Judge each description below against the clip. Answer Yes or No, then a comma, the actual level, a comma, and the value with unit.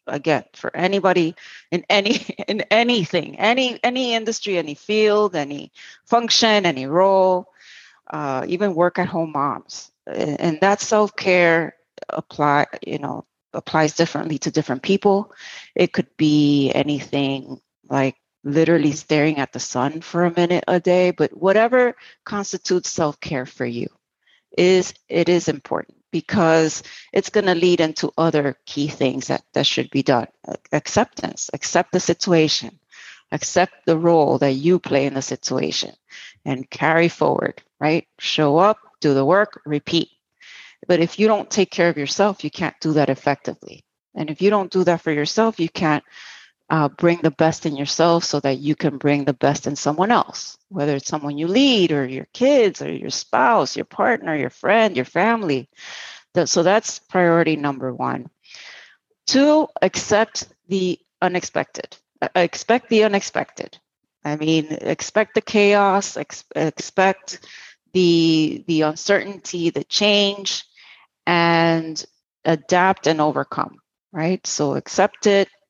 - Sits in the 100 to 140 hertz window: No, medium, 170 Hz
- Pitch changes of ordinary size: Yes, average, 4.8 semitones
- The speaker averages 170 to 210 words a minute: No, average, 145 wpm